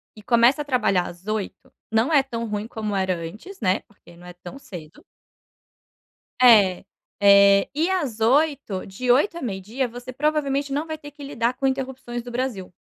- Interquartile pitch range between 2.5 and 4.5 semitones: No, wide, 5.6 semitones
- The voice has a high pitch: Yes, high, 235 Hz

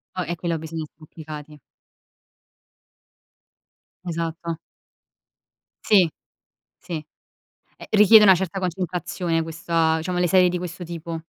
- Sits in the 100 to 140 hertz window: No, medium, 170 Hz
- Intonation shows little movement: Yes, narrow, 2.0 semitones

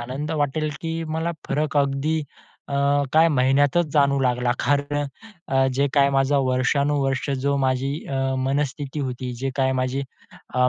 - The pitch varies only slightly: Yes, narrow, 1.7 semitones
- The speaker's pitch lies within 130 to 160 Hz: Yes, medium, 140 Hz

